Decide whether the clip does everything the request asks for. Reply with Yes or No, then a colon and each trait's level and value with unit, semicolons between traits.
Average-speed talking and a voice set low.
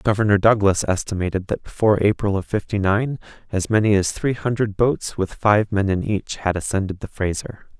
Yes: average, 185 wpm; low, 100 Hz